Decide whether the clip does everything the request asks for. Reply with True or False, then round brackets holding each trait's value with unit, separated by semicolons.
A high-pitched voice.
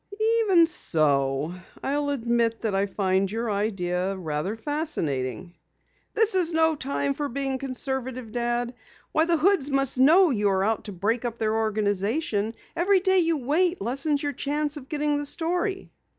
True (260 Hz)